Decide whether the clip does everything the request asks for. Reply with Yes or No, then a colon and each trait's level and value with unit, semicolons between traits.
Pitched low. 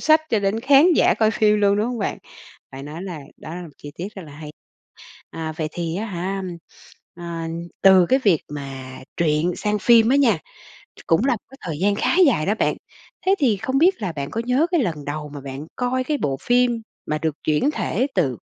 No: high, 195 Hz